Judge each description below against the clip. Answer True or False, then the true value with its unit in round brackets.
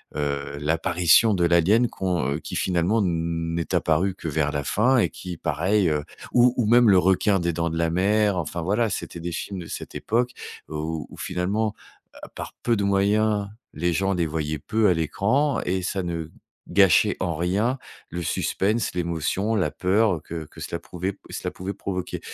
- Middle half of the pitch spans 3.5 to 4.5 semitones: True (3.8 semitones)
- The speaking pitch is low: True (90 Hz)